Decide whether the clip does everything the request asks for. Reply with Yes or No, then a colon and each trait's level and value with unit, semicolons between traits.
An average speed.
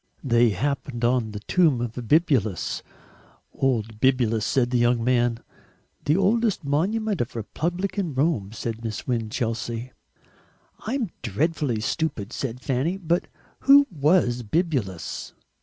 No: slow, 120 wpm